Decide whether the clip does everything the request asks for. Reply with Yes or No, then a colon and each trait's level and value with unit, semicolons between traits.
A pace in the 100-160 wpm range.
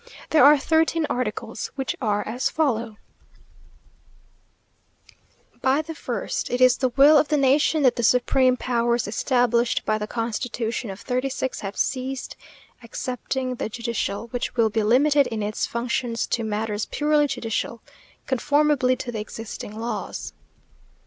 Yes: average, 140 wpm